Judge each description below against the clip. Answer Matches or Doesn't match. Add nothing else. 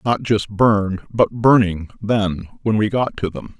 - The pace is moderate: Matches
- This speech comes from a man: Matches